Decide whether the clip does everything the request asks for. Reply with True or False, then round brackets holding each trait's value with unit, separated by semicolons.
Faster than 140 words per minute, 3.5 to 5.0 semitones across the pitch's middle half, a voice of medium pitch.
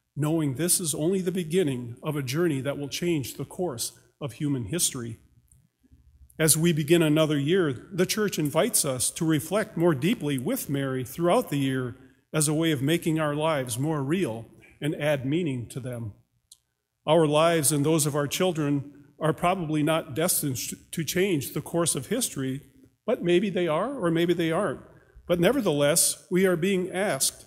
True (175 wpm; 4.0 semitones; 155 Hz)